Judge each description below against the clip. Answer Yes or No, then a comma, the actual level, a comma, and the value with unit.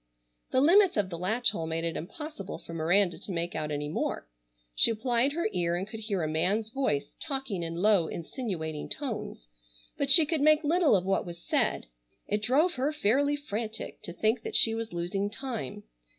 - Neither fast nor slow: Yes, average, 195 wpm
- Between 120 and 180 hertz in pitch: No, high, 210 Hz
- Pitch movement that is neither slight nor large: No, wide, 7.8 semitones